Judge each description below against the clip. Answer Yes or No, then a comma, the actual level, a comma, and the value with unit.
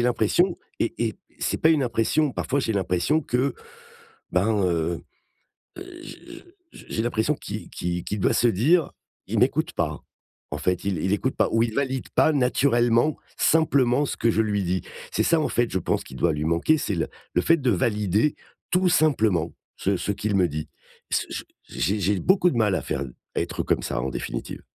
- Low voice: Yes, low, 110 Hz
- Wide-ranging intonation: Yes, wide, 7.2 semitones